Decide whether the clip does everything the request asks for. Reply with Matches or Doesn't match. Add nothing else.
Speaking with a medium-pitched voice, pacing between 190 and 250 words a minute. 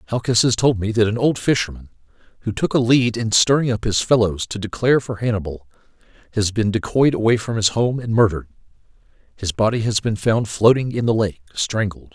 Doesn't match